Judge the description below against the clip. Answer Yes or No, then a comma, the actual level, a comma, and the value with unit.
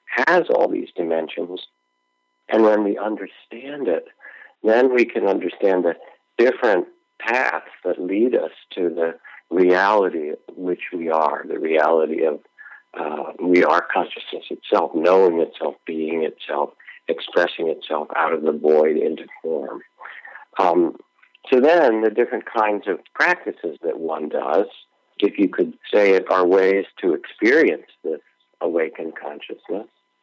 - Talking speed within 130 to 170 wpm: Yes, slow, 135 wpm